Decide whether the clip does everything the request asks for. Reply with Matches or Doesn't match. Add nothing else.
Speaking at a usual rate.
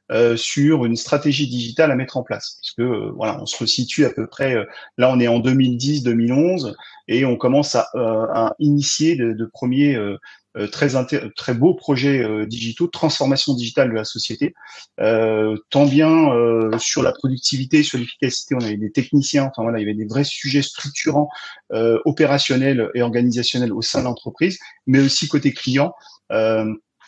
Matches